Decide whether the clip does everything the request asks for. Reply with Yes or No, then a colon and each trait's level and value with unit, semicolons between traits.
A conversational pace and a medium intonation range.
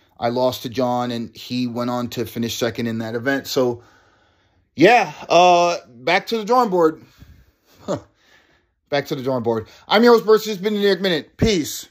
No: average, 185 wpm; wide, 6.9 semitones